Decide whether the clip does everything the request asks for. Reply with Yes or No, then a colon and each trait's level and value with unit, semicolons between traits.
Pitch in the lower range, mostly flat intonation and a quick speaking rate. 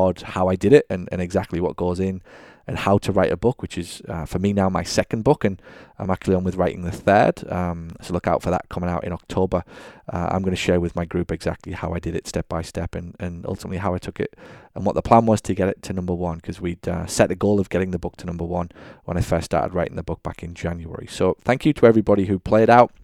Yes: very low, 90 Hz; narrow, 2.3 semitones; fast, 280 wpm